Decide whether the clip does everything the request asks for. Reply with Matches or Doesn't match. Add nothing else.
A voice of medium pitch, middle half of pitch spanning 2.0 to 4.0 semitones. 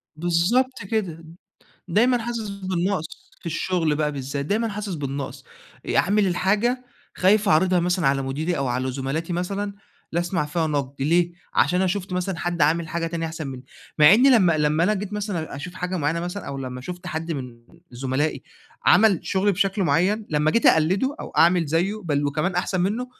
Doesn't match